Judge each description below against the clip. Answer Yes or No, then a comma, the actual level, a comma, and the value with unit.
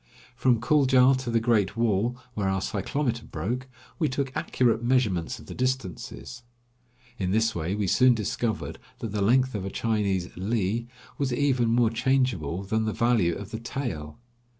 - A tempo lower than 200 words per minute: Yes, average, 165 wpm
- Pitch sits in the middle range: No, low, 115 Hz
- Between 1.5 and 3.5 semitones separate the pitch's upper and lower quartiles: No, average, 4.4 semitones